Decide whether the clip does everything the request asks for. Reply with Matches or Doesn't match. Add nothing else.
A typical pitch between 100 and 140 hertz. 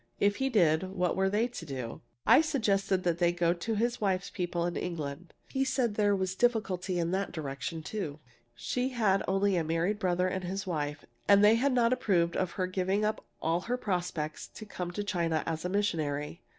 Doesn't match